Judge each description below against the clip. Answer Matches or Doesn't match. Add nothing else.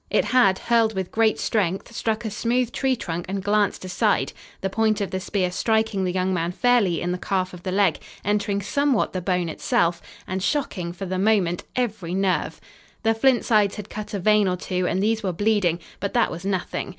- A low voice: Doesn't match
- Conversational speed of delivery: Doesn't match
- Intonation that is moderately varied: Matches